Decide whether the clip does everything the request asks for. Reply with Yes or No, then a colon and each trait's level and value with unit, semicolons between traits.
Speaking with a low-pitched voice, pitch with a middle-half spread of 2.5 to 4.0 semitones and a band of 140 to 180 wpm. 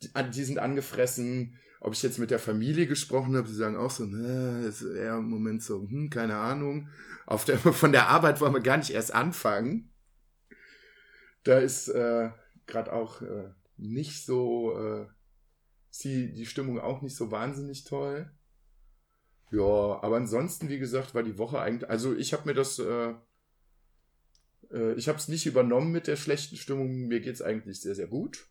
Yes: low, 125 Hz; average, 3.6 semitones; average, 175 wpm